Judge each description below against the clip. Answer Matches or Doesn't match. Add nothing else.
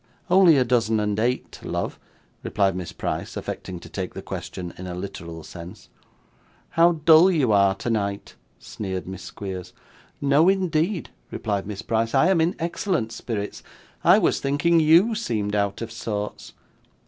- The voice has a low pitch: Matches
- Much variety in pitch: Matches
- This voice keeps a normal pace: Matches